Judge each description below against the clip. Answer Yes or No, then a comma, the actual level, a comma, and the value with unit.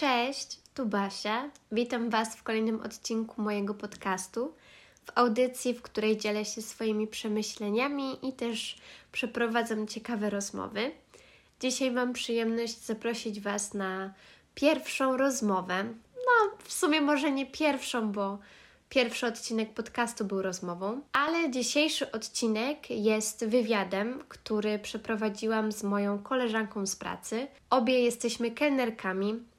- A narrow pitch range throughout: No, average, 3.1 semitones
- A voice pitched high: Yes, high, 230 Hz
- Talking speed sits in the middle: Yes, average, 120 wpm